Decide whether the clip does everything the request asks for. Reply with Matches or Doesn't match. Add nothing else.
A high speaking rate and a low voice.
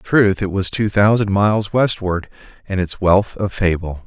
Doesn't match